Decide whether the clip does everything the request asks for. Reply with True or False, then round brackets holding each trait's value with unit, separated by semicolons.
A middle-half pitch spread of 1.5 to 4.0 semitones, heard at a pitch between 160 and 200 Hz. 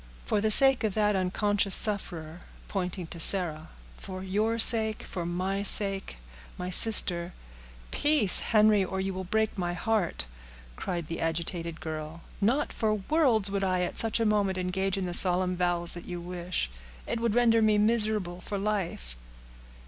True (3.4 semitones; 190 Hz)